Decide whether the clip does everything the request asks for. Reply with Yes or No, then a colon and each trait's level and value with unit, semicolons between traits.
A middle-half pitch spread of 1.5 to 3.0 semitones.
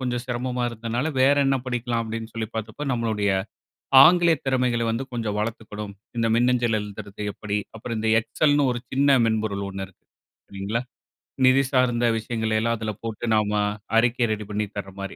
Yes: narrow, 2.5 semitones